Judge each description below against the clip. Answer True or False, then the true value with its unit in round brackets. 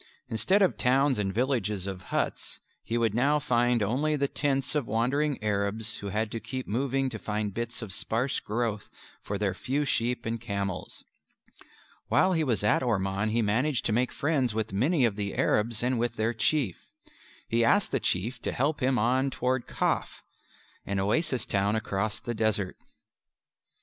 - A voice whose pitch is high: False (115 Hz)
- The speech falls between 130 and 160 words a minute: False (175 wpm)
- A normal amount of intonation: True (4.0 semitones)